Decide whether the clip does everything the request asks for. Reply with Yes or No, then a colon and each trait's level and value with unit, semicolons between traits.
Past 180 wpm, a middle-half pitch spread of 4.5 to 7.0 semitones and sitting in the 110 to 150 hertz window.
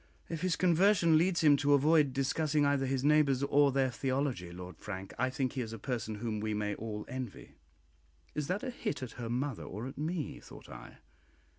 Yes: average, 200 wpm; average, 4.9 semitones; low, 135 Hz